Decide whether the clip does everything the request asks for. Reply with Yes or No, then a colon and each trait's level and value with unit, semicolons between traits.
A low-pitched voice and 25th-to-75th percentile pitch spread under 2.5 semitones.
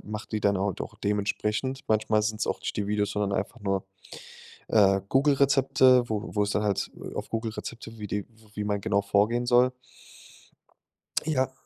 No: low, 105 Hz; average, 2.9 semitones